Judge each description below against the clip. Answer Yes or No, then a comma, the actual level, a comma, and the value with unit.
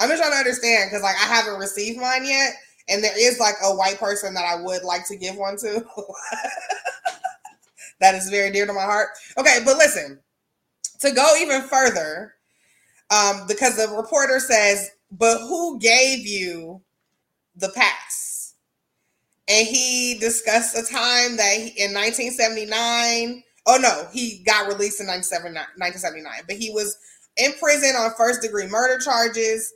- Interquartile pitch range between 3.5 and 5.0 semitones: Yes, average, 3.8 semitones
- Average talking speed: Yes, average, 155 wpm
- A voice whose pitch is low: No, high, 225 Hz